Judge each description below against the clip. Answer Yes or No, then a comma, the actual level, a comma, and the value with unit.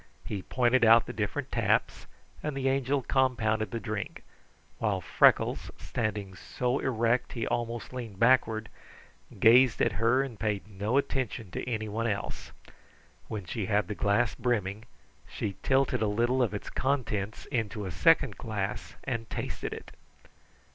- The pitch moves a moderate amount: Yes, average, 3.4 semitones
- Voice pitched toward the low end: Yes, low, 115 Hz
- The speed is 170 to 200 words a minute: No, average, 145 wpm